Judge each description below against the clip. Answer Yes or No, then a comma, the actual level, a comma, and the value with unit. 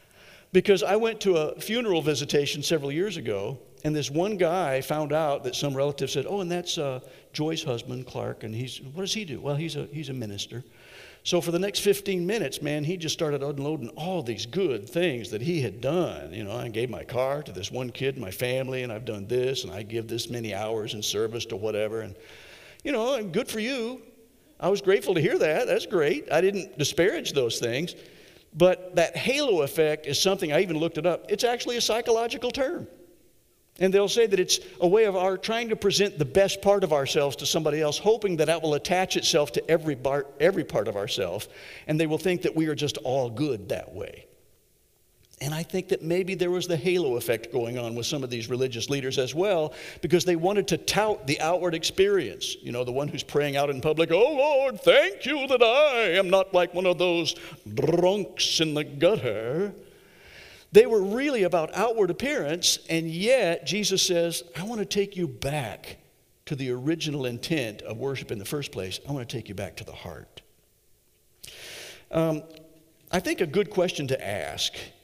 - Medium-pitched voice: Yes, medium, 160 Hz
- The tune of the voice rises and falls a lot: Yes, wide, 6.1 semitones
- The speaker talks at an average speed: No, fast, 210 wpm